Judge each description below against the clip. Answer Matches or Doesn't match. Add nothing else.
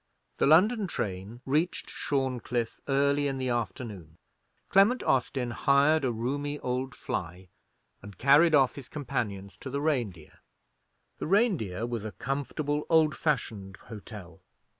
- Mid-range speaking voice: Doesn't match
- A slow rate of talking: Matches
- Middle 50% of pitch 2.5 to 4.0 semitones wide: Doesn't match